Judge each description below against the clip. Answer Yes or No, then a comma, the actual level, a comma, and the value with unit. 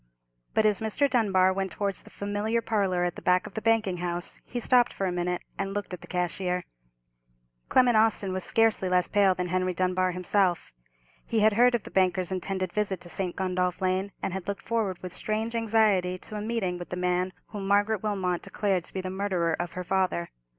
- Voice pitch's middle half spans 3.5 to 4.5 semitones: No, average, 2.7 semitones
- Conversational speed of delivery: No, fast, 210 wpm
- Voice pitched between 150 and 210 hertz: Yes, high, 190 Hz